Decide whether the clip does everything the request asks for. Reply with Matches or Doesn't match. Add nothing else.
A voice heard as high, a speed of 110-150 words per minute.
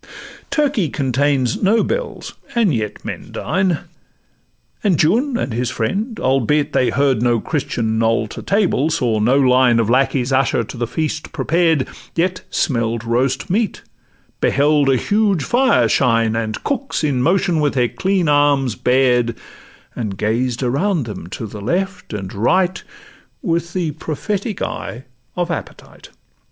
Doesn't match